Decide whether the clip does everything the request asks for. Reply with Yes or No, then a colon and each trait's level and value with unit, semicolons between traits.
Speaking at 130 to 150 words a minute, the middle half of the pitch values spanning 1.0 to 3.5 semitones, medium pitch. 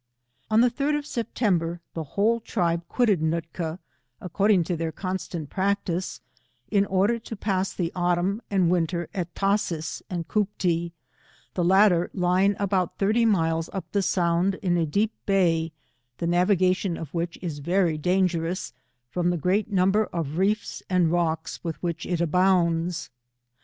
Yes: average, 145 wpm; average, 2.9 semitones; medium, 180 Hz